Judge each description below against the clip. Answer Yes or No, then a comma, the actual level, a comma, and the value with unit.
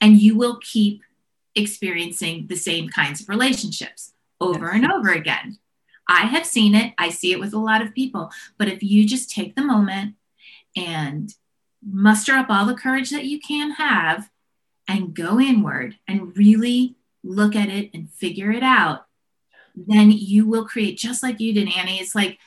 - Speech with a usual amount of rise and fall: Yes, average, 3.6 semitones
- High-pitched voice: Yes, high, 210 Hz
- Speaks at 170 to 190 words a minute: Yes, average, 175 wpm